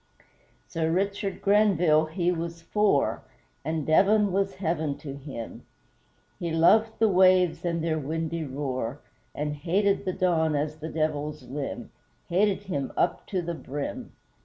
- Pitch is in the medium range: Yes, medium, 165 Hz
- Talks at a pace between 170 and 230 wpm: No, average, 140 wpm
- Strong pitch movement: No, average, 3.7 semitones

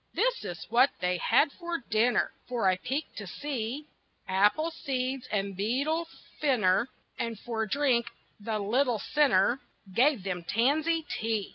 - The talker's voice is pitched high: Yes, high, 240 Hz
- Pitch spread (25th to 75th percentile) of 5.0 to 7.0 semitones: Yes, wide, 5.5 semitones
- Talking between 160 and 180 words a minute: No, average, 140 wpm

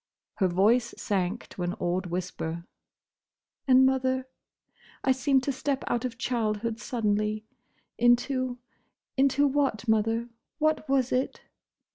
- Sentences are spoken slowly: Yes, slow, 100 wpm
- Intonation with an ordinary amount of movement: Yes, average, 3.7 semitones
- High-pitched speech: Yes, high, 240 Hz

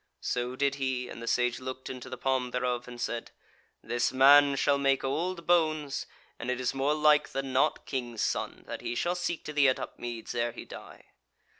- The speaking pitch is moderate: No, low, 130 Hz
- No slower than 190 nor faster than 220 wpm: Yes, average, 200 wpm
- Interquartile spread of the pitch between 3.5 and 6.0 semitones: No, narrow, 2.6 semitones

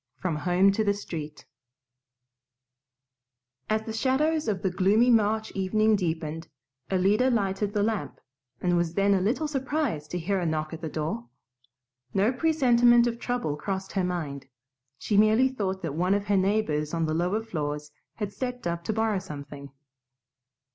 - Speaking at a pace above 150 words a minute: Yes, average, 160 wpm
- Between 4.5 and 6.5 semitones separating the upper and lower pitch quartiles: Yes, average, 5.1 semitones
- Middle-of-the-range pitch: No, high, 195 Hz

